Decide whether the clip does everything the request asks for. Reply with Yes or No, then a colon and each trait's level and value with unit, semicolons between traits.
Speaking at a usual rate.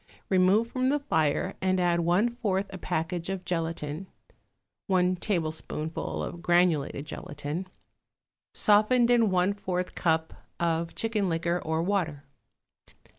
No: slow, 125 wpm